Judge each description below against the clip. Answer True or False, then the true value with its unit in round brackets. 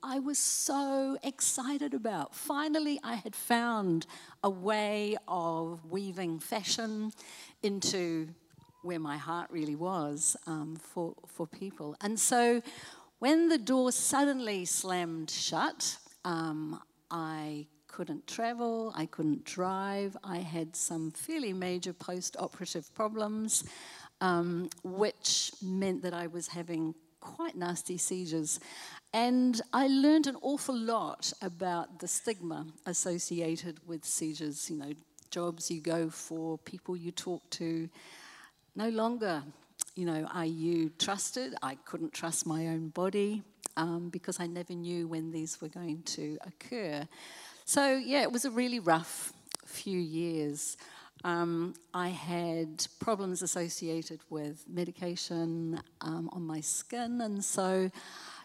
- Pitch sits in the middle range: True (175 Hz)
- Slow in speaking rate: True (130 wpm)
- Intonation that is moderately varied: True (4.8 semitones)